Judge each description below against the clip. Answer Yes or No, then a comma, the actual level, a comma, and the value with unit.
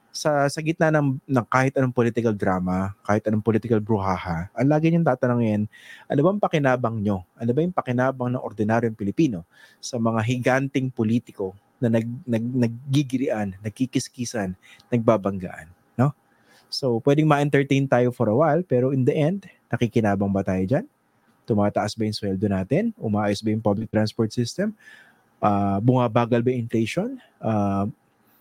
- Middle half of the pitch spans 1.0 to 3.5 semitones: No, average, 4.1 semitones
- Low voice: Yes, low, 120 Hz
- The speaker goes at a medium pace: Yes, average, 150 wpm